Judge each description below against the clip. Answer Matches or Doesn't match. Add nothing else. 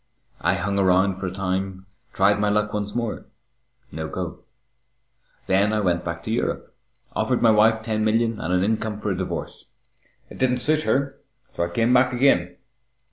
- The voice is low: Matches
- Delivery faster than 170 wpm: Matches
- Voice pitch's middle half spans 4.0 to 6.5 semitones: Doesn't match